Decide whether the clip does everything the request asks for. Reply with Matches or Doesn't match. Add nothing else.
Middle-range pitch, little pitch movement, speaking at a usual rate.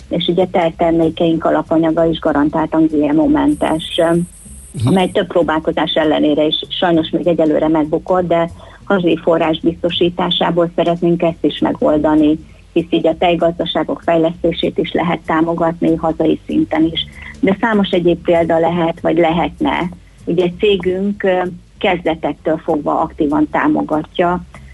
Matches